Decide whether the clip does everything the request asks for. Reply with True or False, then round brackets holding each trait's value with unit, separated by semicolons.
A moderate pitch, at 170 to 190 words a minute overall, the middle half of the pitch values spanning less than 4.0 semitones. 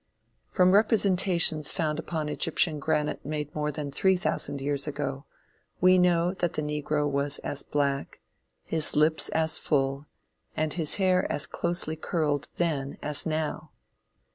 False (155 Hz; 140 wpm; 2.7 semitones)